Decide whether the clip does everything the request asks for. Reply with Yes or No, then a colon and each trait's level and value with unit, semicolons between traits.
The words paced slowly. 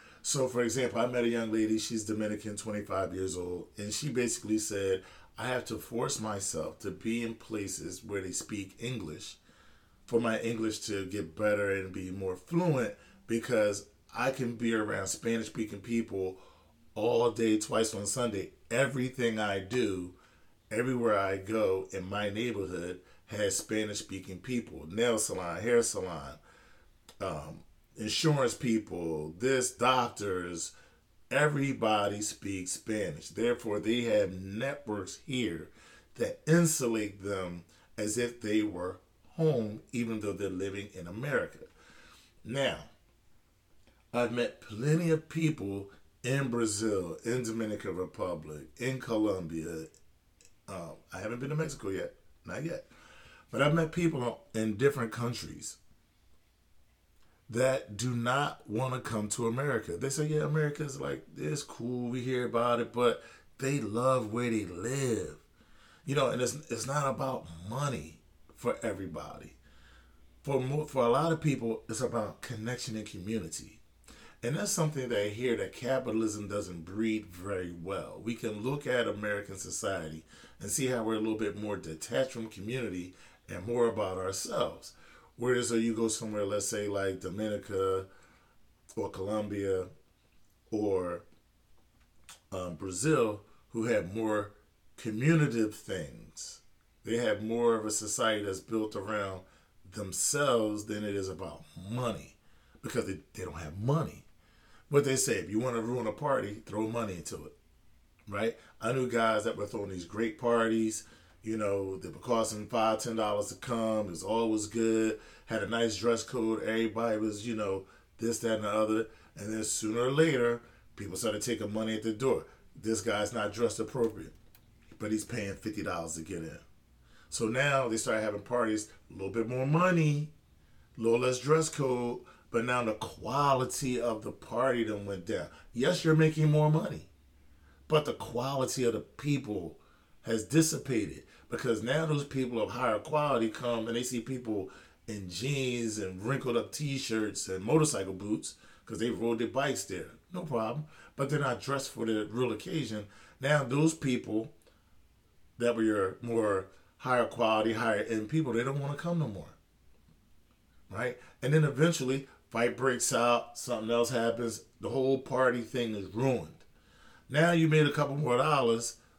No: average, 155 wpm